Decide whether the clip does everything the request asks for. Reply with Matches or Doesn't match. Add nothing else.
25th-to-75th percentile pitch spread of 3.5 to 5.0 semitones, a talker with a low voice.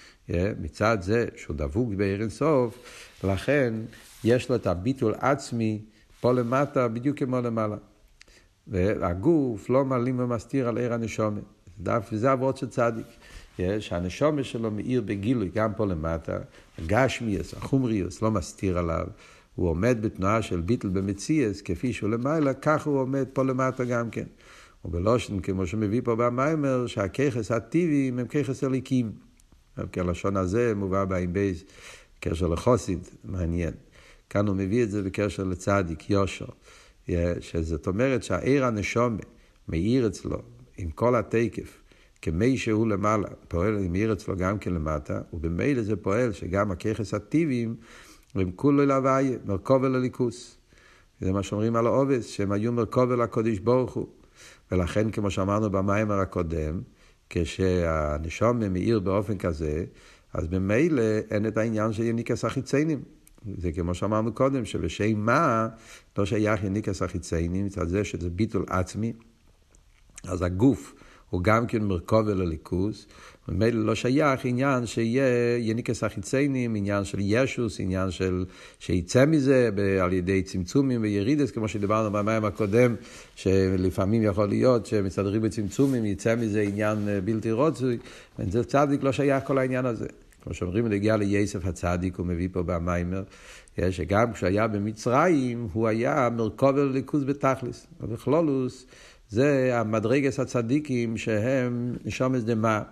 Matches